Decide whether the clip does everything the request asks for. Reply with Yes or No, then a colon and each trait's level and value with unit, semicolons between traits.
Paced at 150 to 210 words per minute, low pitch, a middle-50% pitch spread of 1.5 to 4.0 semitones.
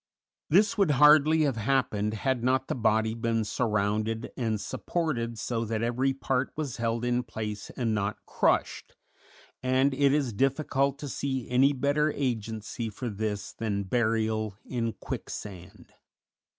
No: average, 140 wpm; low, 120 Hz; average, 3.7 semitones